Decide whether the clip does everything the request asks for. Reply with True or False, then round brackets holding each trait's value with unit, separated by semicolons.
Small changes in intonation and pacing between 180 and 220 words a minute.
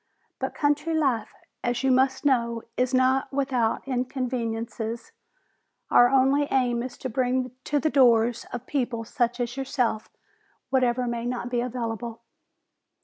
False (2.0 semitones; 140 wpm)